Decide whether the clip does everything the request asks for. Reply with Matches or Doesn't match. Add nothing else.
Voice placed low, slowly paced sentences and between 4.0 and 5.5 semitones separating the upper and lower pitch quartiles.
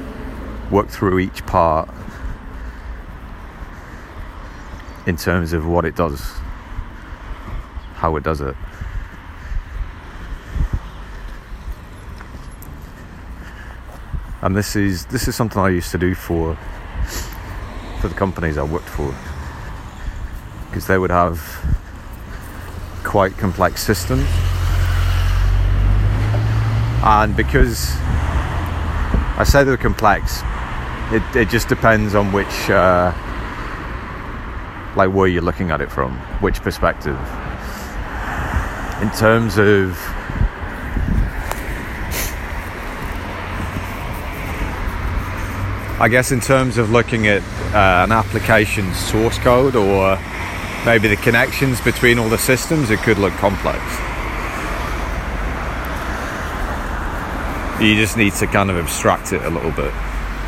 Matches